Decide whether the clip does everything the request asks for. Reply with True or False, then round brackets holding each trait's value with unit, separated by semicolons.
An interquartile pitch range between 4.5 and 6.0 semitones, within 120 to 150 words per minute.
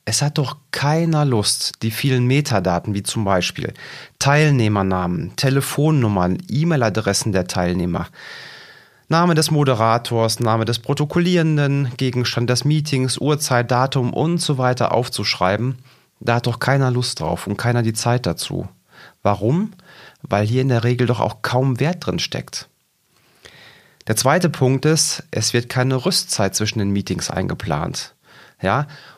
True (4.8 semitones; 140 wpm)